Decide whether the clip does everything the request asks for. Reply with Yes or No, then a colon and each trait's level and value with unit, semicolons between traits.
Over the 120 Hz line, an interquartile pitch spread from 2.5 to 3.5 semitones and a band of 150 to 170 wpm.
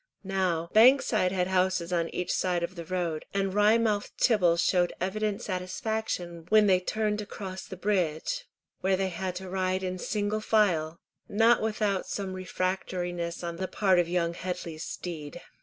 Yes: medium, 185 Hz; average, 2.8 semitones; average, 165 wpm